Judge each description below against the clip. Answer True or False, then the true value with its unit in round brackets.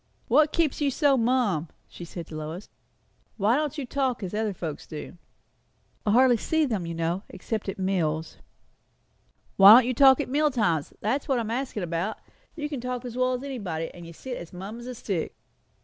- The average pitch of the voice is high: True (225 Hz)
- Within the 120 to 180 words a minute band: False (205 wpm)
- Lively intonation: True (6.7 semitones)